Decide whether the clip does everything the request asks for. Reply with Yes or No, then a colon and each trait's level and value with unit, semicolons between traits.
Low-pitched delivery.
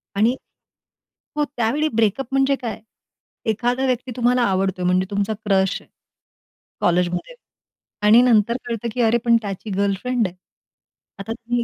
No: high, 230 Hz